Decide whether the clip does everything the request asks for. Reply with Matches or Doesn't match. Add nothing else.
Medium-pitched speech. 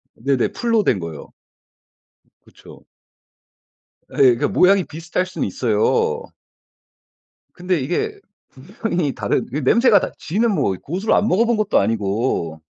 Matches